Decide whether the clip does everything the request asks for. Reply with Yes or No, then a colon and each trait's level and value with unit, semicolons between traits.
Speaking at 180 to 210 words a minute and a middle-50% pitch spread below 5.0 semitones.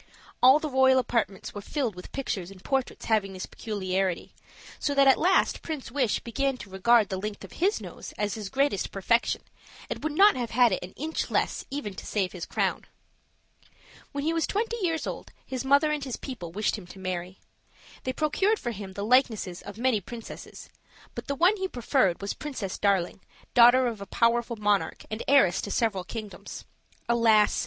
No: average, 190 wpm; wide, 5.6 semitones